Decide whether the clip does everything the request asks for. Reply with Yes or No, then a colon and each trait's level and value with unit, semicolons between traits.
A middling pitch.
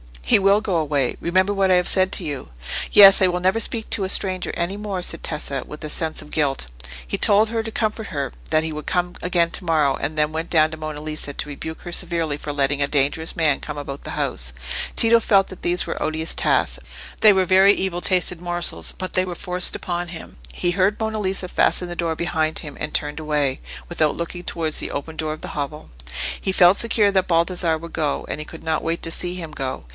Yes: medium, 170 Hz